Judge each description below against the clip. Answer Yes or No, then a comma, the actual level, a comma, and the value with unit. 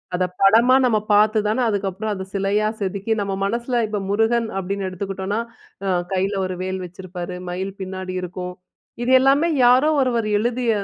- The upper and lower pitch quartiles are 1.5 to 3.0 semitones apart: No, average, 3.4 semitones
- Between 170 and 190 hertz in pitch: No, high, 200 Hz